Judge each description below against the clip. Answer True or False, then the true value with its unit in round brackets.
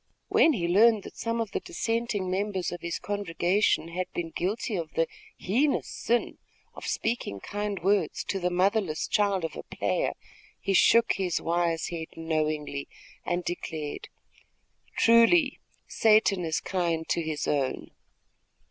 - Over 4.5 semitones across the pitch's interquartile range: False (4.2 semitones)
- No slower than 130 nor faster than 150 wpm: True (145 wpm)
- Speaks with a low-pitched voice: False (185 Hz)